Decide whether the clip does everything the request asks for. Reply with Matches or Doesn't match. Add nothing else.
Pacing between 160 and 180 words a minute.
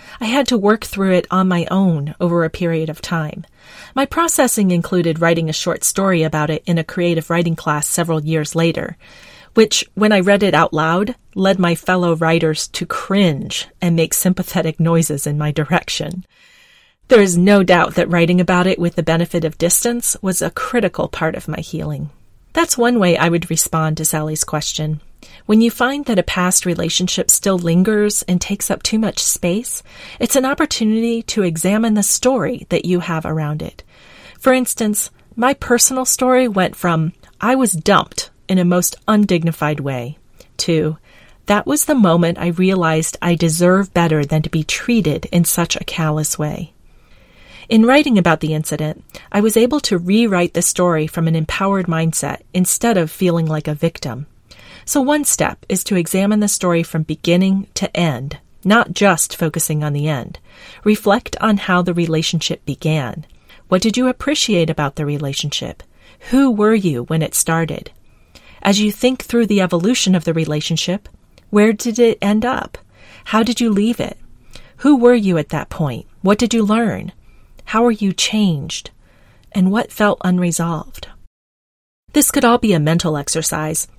Matches